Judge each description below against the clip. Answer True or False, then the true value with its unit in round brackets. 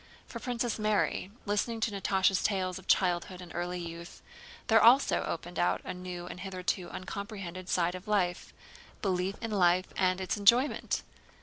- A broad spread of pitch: False (2.5 semitones)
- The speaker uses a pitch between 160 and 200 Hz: True (185 Hz)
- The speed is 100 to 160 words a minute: True (155 wpm)